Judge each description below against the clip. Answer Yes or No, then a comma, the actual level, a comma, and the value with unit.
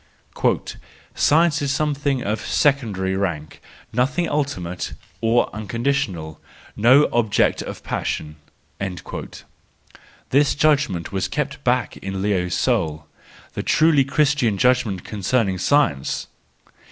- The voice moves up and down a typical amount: No, wide, 6.9 semitones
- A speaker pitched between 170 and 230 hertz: No, low, 120 Hz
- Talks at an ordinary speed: No, slow, 105 wpm